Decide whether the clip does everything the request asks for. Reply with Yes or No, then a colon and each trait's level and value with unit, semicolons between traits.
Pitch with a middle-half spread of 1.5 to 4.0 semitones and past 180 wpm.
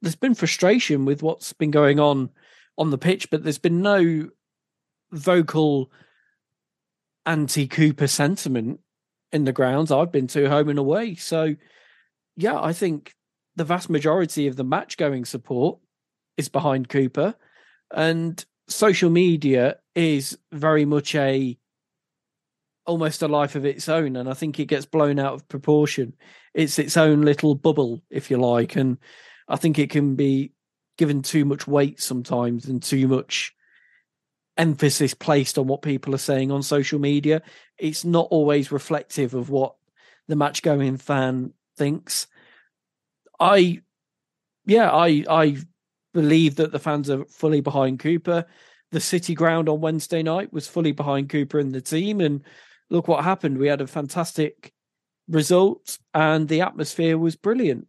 No: average, 2.7 semitones; average, 150 wpm